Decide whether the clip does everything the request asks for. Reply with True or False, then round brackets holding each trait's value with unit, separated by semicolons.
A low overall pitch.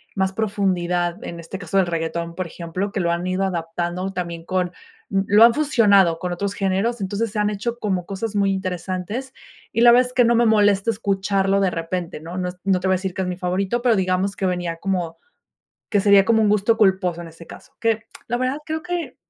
False (195 Hz)